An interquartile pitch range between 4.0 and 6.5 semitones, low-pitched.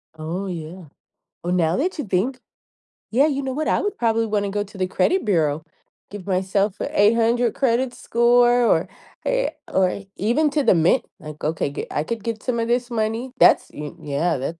No: wide, 5.4 semitones; high, 210 Hz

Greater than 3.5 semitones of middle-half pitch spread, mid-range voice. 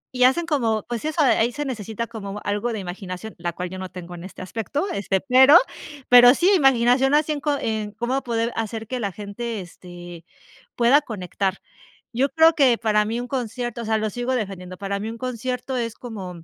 No: average, 4.1 semitones; high, 230 Hz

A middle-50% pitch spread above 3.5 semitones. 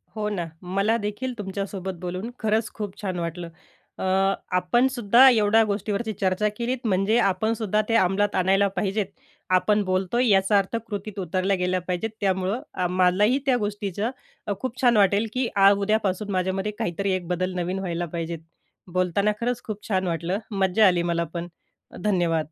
No: average, 2.7 semitones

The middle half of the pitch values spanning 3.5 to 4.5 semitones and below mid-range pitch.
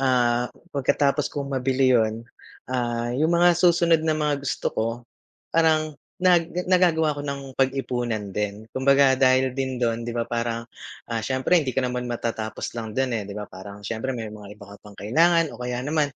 Yes: average, 3.9 semitones; low, 130 Hz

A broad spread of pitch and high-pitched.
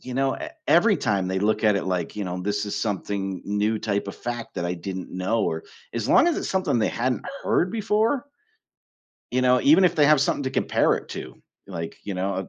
No: wide, 6.2 semitones; low, 105 Hz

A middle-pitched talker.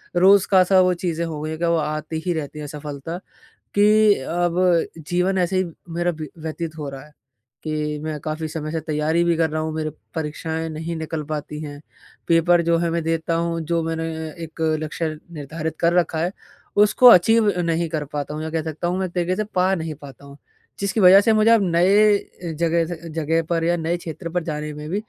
Yes: medium, 165 Hz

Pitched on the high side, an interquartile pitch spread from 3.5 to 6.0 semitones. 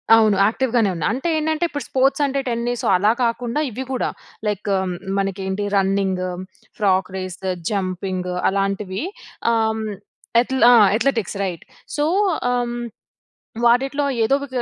Yes: high, 220 Hz; average, 5.0 semitones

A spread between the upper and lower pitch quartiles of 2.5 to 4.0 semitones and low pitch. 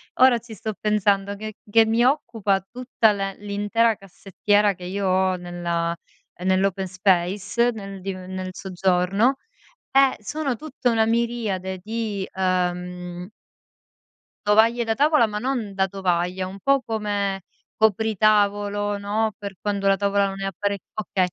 No: average, 2.8 semitones; high, 200 Hz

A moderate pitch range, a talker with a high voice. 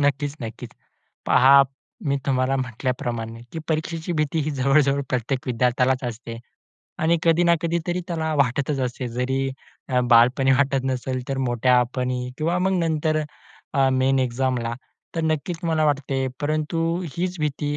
No: average, 3.5 semitones; low, 135 Hz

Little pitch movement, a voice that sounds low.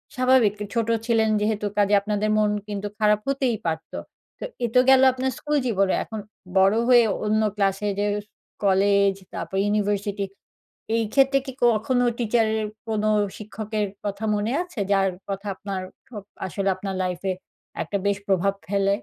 No: narrow, 2.3 semitones; high, 210 Hz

